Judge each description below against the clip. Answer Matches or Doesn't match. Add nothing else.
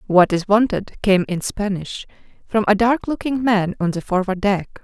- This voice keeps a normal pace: Matches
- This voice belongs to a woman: Matches